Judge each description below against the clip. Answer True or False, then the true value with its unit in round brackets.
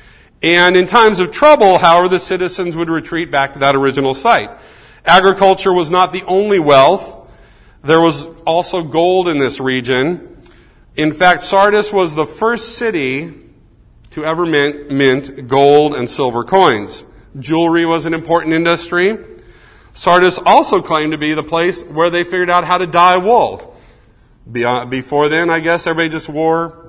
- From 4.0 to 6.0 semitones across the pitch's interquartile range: False (3.5 semitones)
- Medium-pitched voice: True (165 Hz)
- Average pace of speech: True (155 wpm)